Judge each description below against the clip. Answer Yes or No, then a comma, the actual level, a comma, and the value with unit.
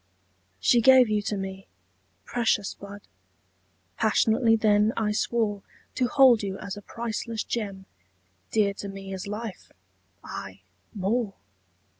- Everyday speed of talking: No, slow, 125 wpm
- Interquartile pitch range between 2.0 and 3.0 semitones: Yes, narrow, 2.6 semitones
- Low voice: No, high, 210 Hz